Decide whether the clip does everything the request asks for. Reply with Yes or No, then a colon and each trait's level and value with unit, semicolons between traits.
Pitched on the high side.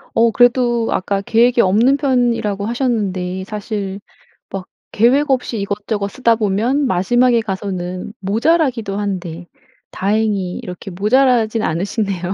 Yes: high, 215 Hz